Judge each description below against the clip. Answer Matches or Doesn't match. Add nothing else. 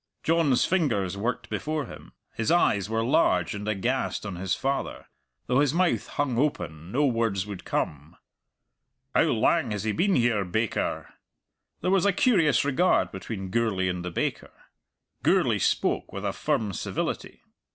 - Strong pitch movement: Matches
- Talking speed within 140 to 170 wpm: Matches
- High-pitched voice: Doesn't match